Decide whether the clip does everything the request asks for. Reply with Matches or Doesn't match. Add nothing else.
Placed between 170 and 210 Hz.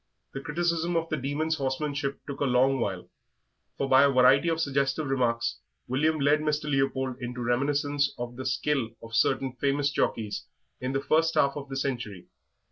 Doesn't match